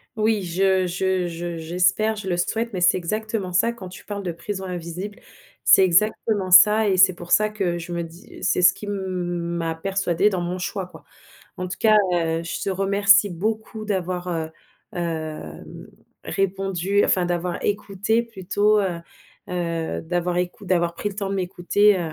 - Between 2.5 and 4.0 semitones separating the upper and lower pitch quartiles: Yes, average, 2.8 semitones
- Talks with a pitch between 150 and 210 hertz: Yes, medium, 185 Hz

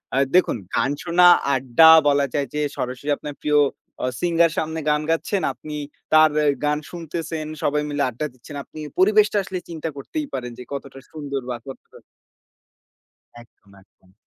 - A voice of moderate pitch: Yes, medium, 150 Hz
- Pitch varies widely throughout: No, average, 3.4 semitones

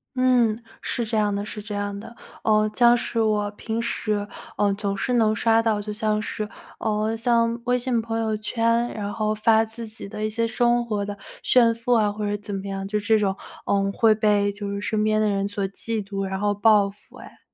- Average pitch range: No, narrow, 1.9 semitones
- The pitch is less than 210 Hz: No, high, 215 Hz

